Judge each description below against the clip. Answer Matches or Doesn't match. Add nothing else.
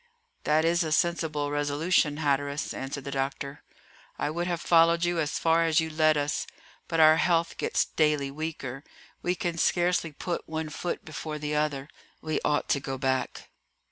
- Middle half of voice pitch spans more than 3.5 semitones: Doesn't match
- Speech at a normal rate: Matches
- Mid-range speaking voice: Matches